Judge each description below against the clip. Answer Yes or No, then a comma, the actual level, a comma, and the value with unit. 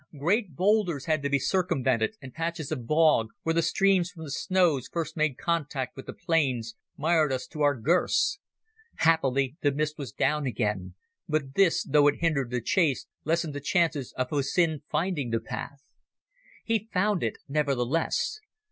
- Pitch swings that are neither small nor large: Yes, average, 3.9 semitones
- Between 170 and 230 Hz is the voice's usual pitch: No, medium, 150 Hz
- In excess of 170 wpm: No, average, 165 wpm